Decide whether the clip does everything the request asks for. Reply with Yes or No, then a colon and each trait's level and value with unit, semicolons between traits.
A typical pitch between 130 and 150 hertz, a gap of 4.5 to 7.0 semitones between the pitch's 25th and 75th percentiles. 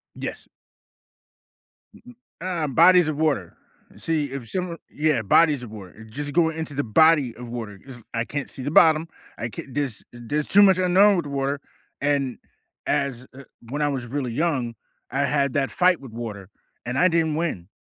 Yes: medium, 140 Hz; average, 4.8 semitones